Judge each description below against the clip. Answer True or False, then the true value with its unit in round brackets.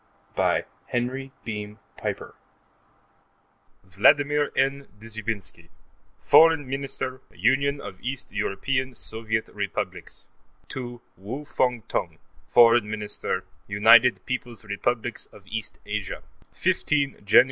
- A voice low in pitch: True (120 Hz)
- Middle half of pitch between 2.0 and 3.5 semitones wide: False (4.2 semitones)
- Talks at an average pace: False (105 wpm)